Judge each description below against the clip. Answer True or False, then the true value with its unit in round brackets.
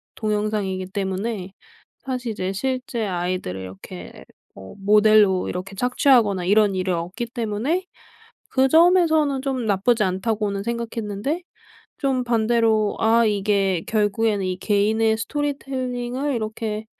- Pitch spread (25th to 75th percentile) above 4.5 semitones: False (4.0 semitones)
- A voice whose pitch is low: False (215 Hz)